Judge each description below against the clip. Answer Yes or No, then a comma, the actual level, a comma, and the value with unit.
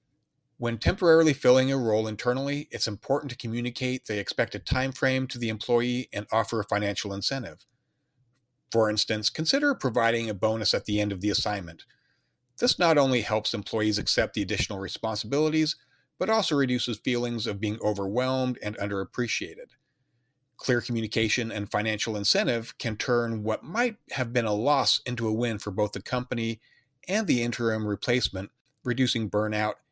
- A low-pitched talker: Yes, low, 115 Hz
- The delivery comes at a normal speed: Yes, average, 155 wpm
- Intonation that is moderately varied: Yes, average, 3.3 semitones